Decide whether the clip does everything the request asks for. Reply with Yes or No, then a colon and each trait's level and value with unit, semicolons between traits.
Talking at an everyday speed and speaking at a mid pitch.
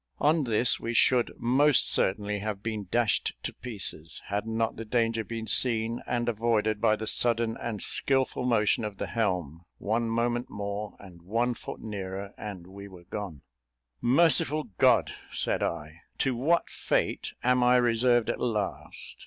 No: average, 160 wpm; low, 115 Hz